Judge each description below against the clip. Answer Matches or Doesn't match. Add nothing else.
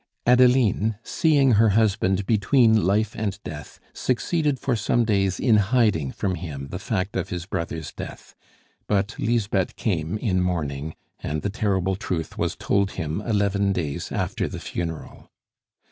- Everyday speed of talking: Matches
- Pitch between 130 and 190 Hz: Doesn't match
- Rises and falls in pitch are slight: Doesn't match